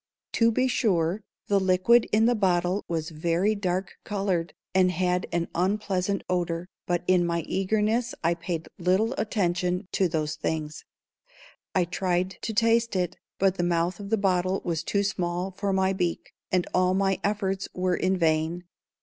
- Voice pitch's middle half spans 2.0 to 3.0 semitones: Yes, narrow, 2.4 semitones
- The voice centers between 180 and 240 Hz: Yes, medium, 185 Hz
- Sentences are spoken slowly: No, average, 165 wpm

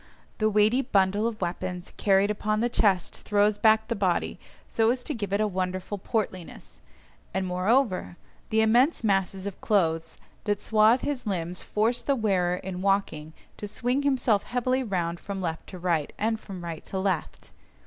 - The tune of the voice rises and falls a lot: No, average, 3.3 semitones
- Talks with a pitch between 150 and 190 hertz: No, high, 200 Hz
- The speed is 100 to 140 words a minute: No, average, 170 wpm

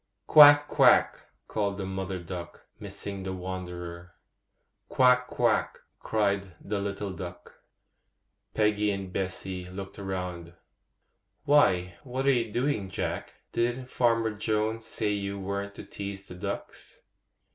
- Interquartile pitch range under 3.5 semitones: Yes, average, 3.1 semitones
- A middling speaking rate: No, slow, 125 wpm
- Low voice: Yes, low, 100 Hz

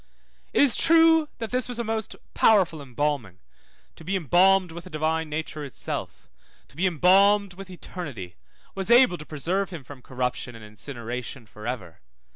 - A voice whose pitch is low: No, medium, 165 Hz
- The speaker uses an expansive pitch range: Yes, wide, 7.0 semitones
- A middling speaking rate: Yes, average, 165 wpm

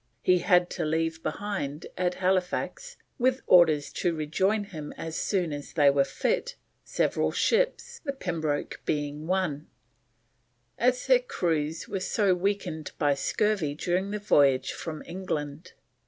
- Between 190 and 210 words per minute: No, average, 140 wpm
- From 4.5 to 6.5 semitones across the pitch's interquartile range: Yes, average, 4.8 semitones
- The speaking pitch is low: No, medium, 175 Hz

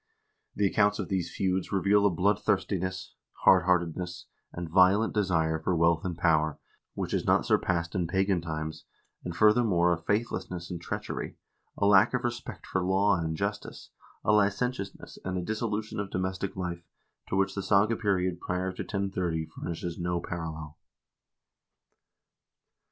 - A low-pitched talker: Yes, very low, 95 Hz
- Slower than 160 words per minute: Yes, average, 145 wpm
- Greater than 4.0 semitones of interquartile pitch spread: No, average, 2.8 semitones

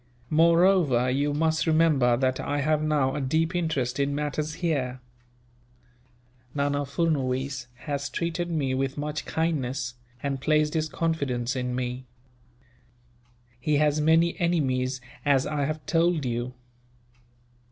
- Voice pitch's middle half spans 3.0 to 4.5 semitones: Yes, average, 3.4 semitones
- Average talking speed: No, slow, 125 wpm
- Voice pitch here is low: No, medium, 145 Hz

